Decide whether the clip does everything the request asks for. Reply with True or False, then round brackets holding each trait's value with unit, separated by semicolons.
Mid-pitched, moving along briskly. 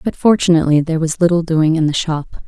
True (165 Hz; 220 wpm)